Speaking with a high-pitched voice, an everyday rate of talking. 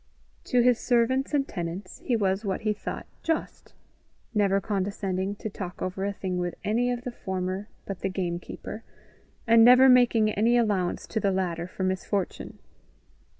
Yes: high, 200 Hz; average, 165 wpm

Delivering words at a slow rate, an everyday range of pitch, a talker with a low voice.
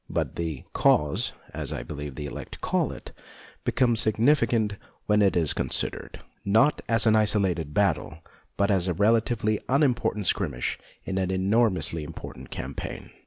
No: average, 155 wpm; average, 4.9 semitones; low, 100 Hz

